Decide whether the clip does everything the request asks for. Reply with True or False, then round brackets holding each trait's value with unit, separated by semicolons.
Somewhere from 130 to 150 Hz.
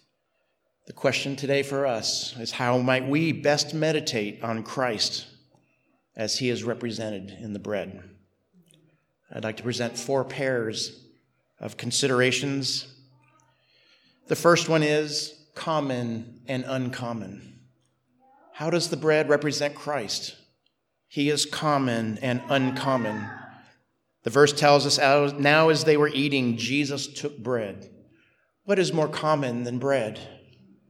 True (135 Hz)